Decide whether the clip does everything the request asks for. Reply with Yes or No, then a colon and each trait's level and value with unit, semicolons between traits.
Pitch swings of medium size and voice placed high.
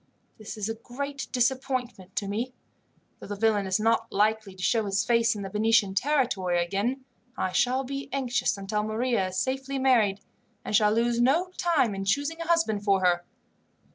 Yes: average, 4.6 semitones; high, 225 Hz